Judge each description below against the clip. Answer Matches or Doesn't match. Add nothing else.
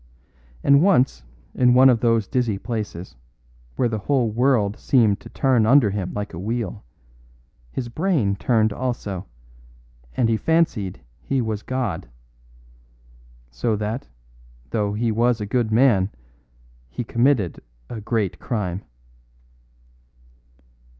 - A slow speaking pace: Matches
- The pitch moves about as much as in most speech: Matches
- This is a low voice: Matches